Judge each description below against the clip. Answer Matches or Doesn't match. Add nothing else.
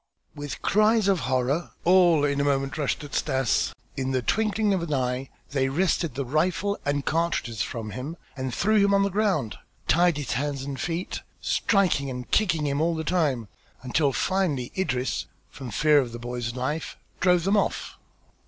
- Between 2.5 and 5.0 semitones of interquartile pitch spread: Doesn't match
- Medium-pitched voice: Matches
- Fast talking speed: Doesn't match